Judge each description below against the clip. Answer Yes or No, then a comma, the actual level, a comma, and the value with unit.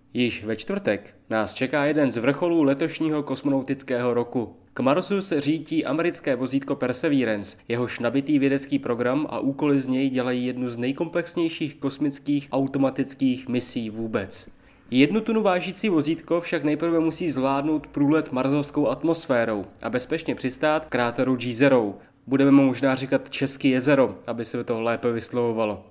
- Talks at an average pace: Yes, average, 145 wpm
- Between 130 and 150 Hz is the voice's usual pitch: Yes, low, 135 Hz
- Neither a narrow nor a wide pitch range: Yes, average, 4.0 semitones